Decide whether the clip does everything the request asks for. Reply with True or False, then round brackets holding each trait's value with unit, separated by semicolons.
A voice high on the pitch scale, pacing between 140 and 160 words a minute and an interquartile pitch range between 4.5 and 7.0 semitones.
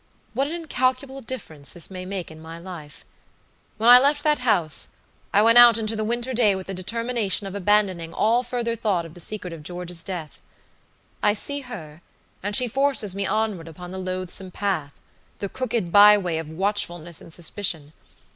False (200 Hz; 180 wpm; 5.1 semitones)